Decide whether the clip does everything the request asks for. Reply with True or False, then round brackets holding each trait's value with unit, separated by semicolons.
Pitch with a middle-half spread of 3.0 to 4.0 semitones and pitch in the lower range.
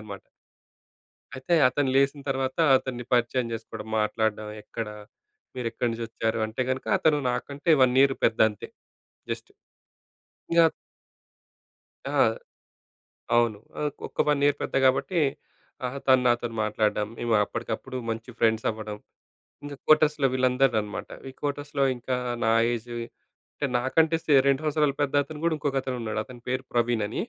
True (3.7 semitones; 125 Hz)